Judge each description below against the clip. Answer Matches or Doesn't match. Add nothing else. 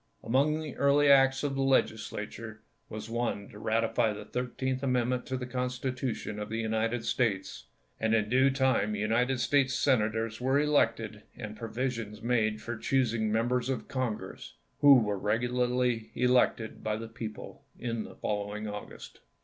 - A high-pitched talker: Doesn't match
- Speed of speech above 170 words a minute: Doesn't match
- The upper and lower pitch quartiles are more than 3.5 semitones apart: Doesn't match